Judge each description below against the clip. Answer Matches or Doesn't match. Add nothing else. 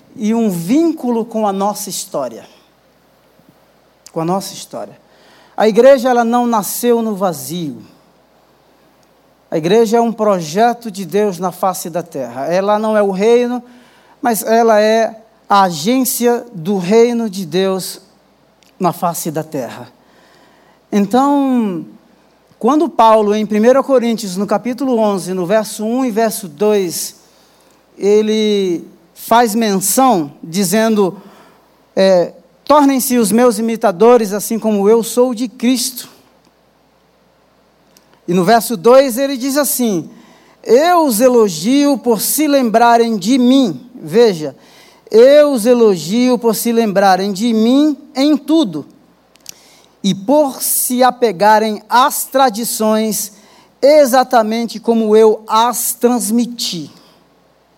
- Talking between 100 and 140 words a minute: Matches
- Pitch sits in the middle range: Doesn't match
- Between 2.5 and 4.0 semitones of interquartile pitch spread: Matches